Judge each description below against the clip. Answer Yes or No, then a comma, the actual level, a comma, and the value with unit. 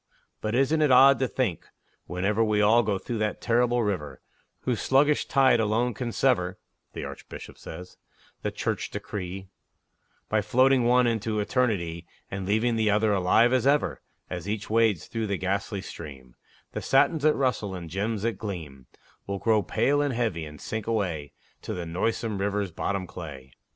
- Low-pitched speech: Yes, low, 105 Hz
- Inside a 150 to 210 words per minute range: Yes, average, 170 wpm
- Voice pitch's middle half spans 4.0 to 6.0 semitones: Yes, average, 4.5 semitones